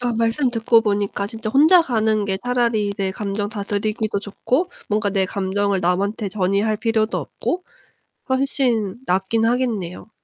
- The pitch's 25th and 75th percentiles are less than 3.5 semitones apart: Yes, average, 2.7 semitones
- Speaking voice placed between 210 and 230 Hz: Yes, high, 215 Hz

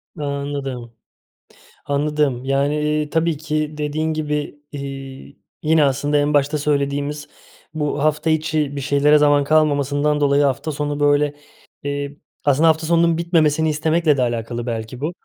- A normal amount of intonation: No, narrow, 1.4 semitones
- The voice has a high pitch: No, medium, 145 Hz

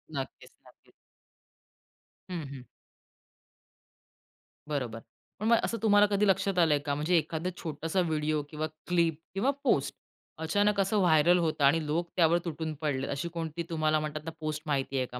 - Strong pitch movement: No, average, 3.0 semitones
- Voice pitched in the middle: Yes, medium, 160 Hz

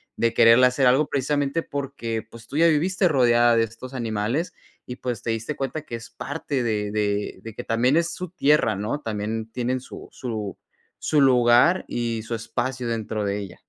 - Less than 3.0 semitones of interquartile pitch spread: No, average, 3.7 semitones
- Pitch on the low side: Yes, low, 120 Hz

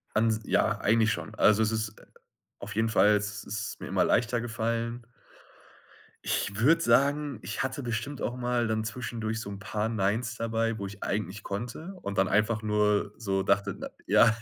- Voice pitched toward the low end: Yes, low, 110 Hz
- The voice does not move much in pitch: Yes, narrow, 2.0 semitones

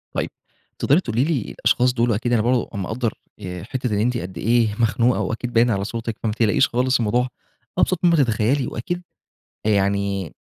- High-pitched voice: No, low, 115 Hz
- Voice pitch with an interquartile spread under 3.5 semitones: Yes, average, 2.8 semitones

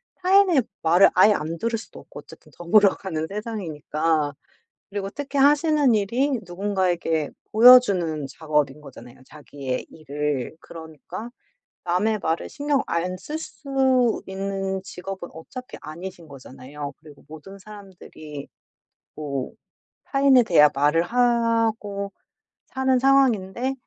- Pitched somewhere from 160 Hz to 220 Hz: Yes, high, 190 Hz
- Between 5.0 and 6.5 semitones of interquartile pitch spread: No, wide, 7.3 semitones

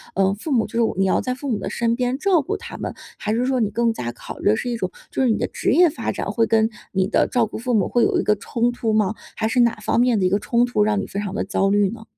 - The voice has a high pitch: Yes, high, 225 Hz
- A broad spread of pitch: No, average, 3.0 semitones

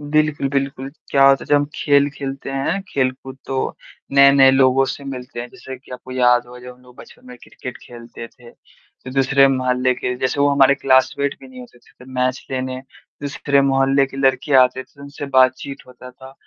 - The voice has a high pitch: No, low, 135 Hz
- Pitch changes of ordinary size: No, narrow, 1.4 semitones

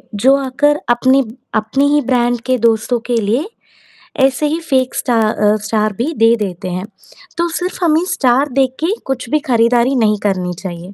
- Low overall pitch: No, high, 245 Hz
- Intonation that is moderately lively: Yes, average, 4.3 semitones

